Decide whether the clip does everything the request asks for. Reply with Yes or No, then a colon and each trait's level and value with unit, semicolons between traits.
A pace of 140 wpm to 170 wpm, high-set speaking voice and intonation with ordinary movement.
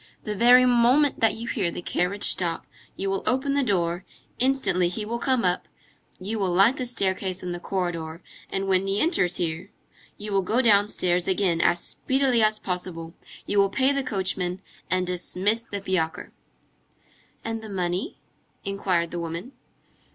Yes: average, 165 wpm; high, 195 Hz; average, 4.3 semitones